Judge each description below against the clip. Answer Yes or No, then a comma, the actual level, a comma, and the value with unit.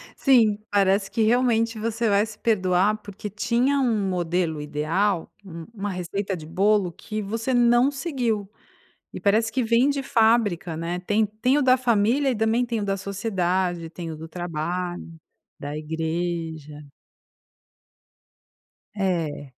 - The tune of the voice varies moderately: Yes, average, 4.7 semitones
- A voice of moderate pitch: No, high, 200 Hz